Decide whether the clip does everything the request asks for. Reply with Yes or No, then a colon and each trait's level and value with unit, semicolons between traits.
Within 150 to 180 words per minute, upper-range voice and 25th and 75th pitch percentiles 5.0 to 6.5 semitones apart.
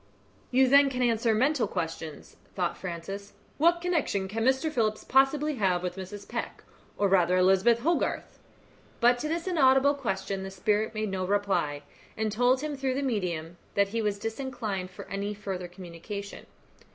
Yes: average, 165 wpm; high, 215 Hz; wide, 5.6 semitones